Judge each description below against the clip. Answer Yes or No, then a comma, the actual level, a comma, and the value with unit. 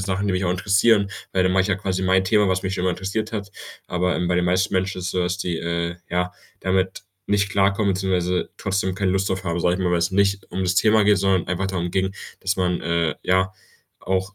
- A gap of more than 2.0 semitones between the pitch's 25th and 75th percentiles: No, narrow, 1.5 semitones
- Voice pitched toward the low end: Yes, very low, 95 Hz